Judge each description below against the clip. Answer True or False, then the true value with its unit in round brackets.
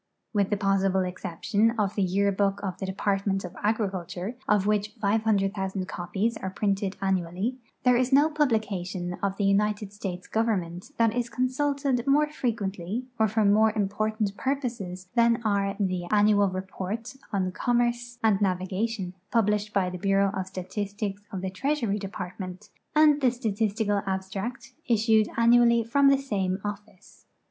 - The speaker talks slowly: False (150 wpm)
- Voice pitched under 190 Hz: False (205 Hz)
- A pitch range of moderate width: True (3.2 semitones)